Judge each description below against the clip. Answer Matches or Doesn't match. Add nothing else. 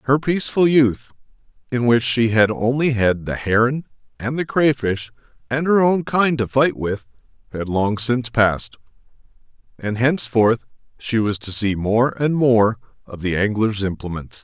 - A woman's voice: Doesn't match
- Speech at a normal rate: Matches